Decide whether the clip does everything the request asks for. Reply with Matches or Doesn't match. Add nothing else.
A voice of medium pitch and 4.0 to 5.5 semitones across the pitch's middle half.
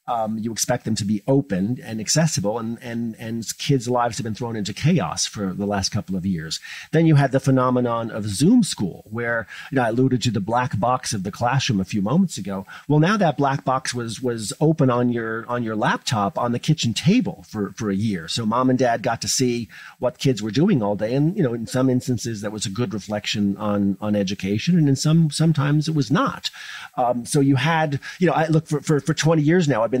Doesn't match